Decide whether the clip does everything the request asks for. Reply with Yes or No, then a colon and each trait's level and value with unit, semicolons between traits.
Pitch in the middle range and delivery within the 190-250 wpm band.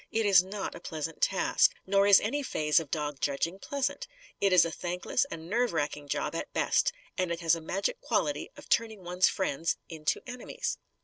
Yes: medium, 180 Hz; average, 195 wpm